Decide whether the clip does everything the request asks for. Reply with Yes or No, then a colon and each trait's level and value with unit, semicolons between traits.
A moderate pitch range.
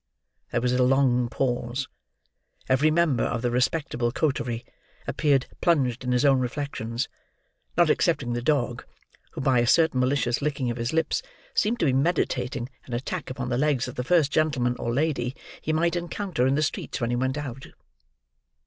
Yes: average, 3.5 semitones